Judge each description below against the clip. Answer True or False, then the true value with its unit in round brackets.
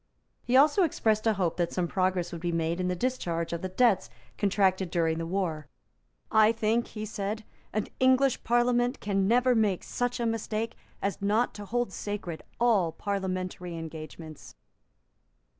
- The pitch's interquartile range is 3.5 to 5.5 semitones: True (4.6 semitones)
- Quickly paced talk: False (160 wpm)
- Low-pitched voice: False (200 Hz)